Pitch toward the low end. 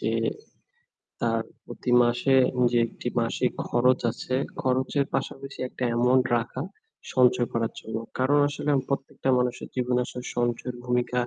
Yes: low, 125 Hz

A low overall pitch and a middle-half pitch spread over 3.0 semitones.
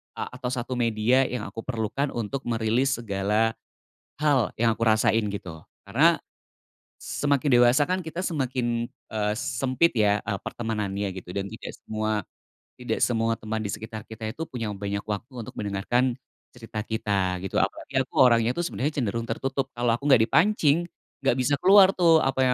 Yes: low, 115 Hz; average, 3.8 semitones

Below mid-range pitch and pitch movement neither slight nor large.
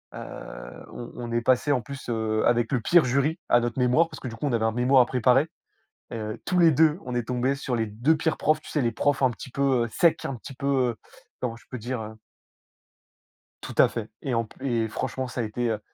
Yes: low, 125 Hz; average, 3.0 semitones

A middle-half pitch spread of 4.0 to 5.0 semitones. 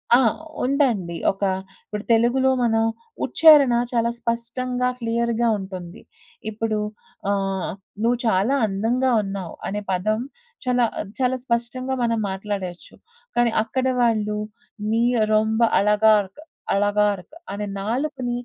No: average, 3.1 semitones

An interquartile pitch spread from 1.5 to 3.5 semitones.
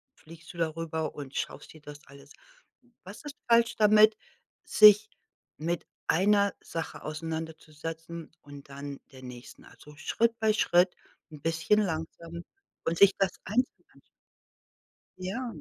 No: average, 5.0 semitones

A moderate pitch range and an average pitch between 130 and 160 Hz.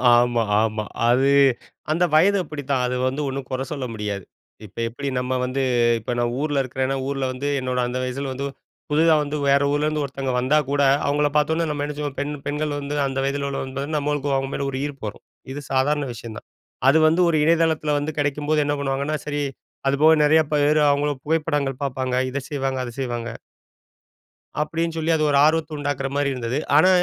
No: narrow, 2.2 semitones; medium, 140 Hz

